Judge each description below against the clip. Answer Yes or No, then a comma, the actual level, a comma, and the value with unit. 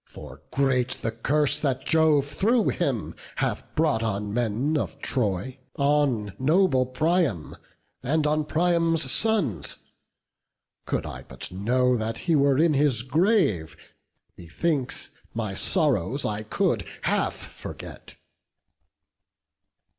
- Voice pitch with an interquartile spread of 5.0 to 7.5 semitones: Yes, wide, 5.5 semitones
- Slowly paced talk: Yes, slow, 115 wpm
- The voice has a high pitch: No, low, 135 Hz